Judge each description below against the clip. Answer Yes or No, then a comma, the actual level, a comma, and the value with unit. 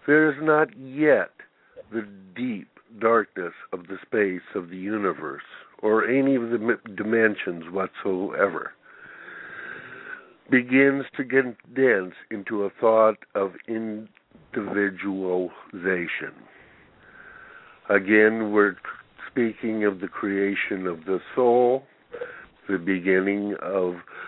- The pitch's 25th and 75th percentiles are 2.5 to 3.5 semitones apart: No, average, 5.1 semitones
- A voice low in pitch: Yes, low, 110 Hz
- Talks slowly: Yes, slow, 100 wpm